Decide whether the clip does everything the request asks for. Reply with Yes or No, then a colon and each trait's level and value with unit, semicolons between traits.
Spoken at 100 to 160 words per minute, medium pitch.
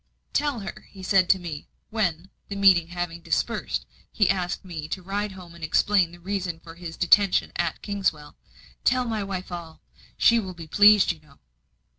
No: average, 180 wpm; medium, 180 Hz